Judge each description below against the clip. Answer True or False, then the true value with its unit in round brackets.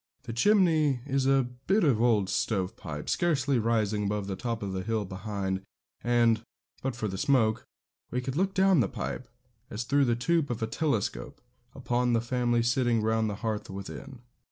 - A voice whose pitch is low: True (120 Hz)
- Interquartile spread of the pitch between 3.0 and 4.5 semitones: True (4.0 semitones)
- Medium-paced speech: True (180 wpm)